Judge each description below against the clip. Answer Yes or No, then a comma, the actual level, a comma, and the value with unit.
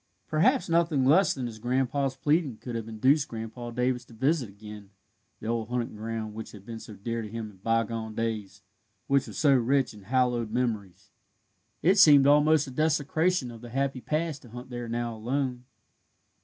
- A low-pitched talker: Yes, low, 120 Hz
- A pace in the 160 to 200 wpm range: Yes, average, 185 wpm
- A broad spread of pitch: No, average, 3.7 semitones